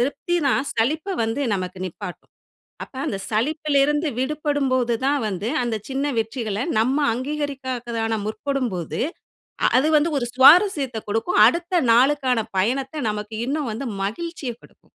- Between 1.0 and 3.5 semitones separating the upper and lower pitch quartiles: No, average, 4.7 semitones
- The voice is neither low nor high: No, very high, 260 Hz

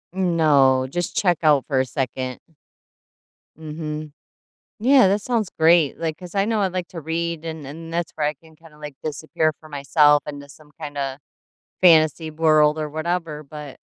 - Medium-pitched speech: Yes, medium, 155 Hz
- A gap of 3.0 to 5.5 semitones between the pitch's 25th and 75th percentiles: No, narrow, 2.4 semitones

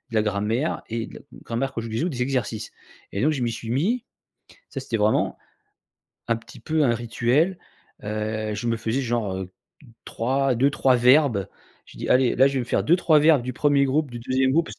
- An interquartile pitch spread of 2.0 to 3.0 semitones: No, average, 3.4 semitones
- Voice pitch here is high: No, low, 125 Hz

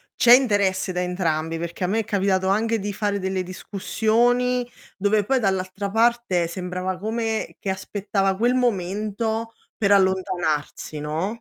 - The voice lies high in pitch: Yes, high, 195 Hz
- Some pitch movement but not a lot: Yes, average, 3.2 semitones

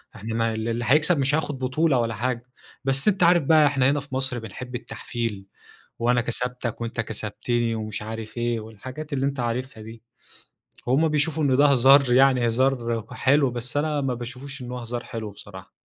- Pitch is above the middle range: No, low, 125 Hz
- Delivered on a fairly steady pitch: No, average, 3.1 semitones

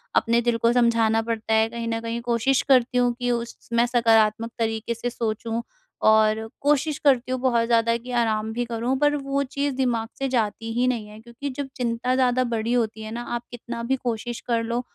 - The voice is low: No, high, 235 Hz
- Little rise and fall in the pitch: Yes, narrow, 1.7 semitones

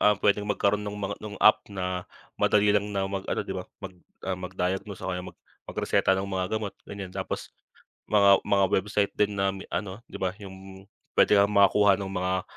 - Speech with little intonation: Yes, narrow, 1.4 semitones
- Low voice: Yes, low, 100 Hz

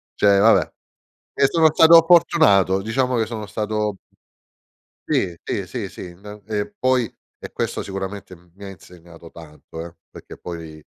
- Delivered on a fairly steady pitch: No, average, 4.4 semitones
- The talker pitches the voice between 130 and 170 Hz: No, low, 100 Hz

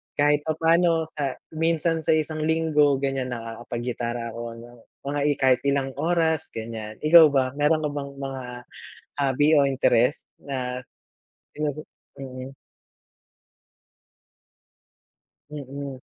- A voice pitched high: No, medium, 140 Hz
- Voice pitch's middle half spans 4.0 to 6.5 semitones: No, average, 3.2 semitones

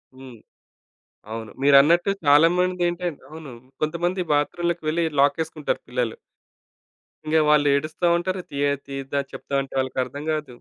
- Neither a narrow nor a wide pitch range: Yes, average, 3.7 semitones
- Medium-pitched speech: Yes, medium, 150 Hz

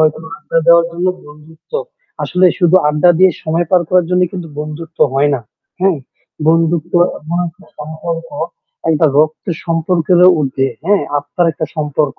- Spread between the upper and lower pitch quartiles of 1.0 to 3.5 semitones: Yes, narrow, 2.4 semitones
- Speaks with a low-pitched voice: No, medium, 165 Hz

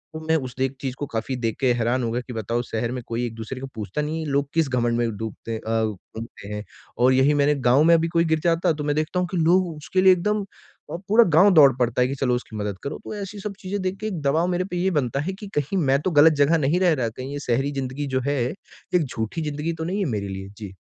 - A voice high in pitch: No, medium, 140 Hz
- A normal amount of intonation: No, wide, 5.7 semitones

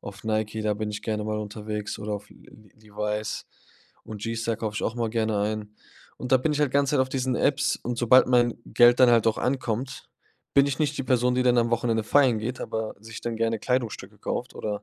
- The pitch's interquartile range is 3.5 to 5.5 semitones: No, average, 2.8 semitones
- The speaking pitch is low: Yes, low, 115 Hz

